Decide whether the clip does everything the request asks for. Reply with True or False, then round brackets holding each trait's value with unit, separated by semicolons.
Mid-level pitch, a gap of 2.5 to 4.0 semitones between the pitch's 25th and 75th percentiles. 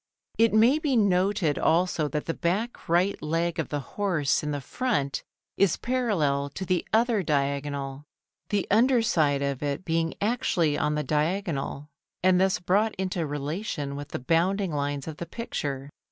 False (165 Hz; 5.6 semitones)